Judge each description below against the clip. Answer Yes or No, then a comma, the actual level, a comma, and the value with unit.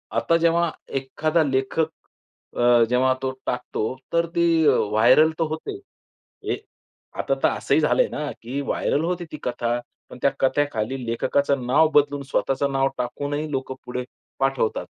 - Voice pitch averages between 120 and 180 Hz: Yes, medium, 140 Hz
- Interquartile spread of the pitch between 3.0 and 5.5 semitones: Yes, average, 4.0 semitones